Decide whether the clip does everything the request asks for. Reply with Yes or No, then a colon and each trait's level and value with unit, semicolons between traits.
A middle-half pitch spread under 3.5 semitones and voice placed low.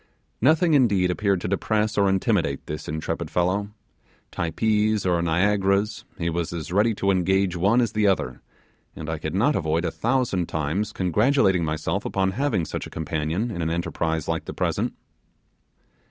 No: average, 4.2 semitones; very low, 95 Hz